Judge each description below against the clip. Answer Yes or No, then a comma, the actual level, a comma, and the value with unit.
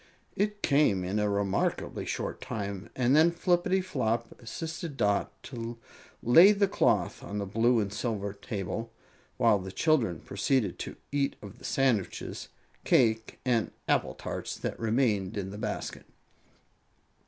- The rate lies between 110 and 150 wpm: Yes, average, 140 wpm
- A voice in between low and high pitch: No, low, 115 Hz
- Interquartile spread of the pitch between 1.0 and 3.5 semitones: No, wide, 5.5 semitones